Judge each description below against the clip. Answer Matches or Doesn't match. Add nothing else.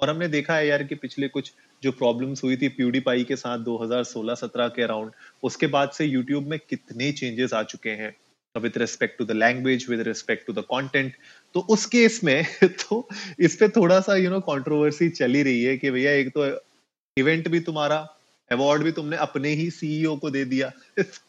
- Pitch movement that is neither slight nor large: Matches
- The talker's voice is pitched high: Doesn't match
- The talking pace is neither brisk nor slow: Doesn't match